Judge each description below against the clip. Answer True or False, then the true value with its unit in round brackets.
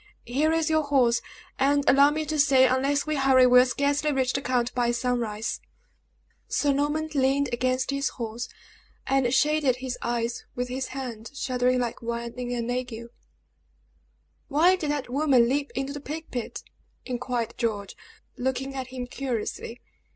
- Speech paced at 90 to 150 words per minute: False (160 wpm)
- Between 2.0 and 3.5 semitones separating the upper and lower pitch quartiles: True (2.6 semitones)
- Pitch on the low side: False (260 Hz)